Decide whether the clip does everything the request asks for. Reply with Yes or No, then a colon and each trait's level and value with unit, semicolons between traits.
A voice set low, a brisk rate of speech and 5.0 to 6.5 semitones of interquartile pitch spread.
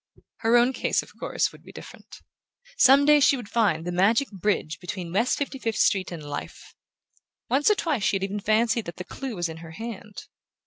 No: high, 210 Hz; fast, 210 wpm; wide, 5.6 semitones